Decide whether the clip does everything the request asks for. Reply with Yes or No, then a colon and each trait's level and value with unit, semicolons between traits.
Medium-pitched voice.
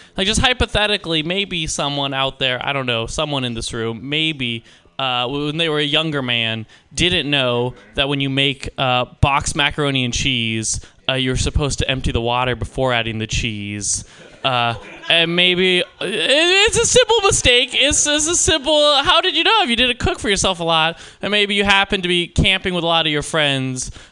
Yes: medium, 145 Hz